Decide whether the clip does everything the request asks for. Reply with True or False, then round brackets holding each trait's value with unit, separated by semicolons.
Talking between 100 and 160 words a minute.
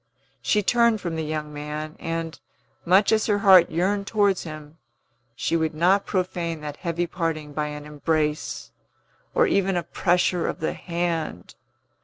True (155 wpm)